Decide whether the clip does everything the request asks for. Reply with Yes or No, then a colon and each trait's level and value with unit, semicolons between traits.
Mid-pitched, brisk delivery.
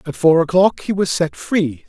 Yes: medium, 165 Hz; fast, 225 wpm